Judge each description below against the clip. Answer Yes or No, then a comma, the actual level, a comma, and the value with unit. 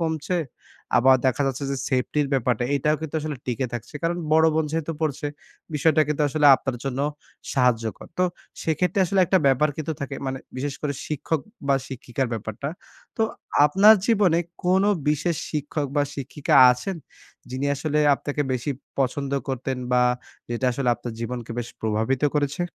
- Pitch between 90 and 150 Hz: Yes, medium, 140 Hz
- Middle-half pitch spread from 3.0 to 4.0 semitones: Yes, average, 3.6 semitones